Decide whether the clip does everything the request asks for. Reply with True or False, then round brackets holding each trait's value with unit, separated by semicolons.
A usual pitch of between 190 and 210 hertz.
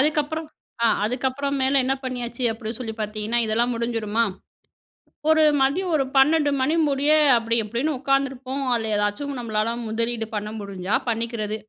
False (240 Hz)